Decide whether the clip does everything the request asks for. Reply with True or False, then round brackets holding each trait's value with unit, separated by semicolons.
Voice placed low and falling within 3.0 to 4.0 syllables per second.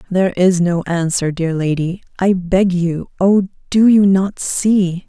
False (185 Hz; 3.7 syllables/s)